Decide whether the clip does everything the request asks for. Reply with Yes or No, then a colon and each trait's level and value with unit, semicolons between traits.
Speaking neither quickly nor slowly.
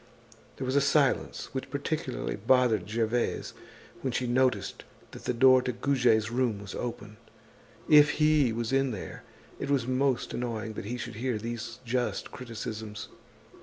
Yes: average, 155 wpm